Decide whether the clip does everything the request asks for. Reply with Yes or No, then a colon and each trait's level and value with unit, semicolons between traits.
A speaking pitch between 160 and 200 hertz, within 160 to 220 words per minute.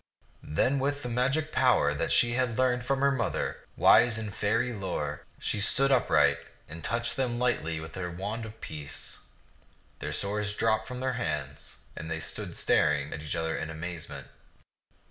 No: low, 110 Hz; average, 170 wpm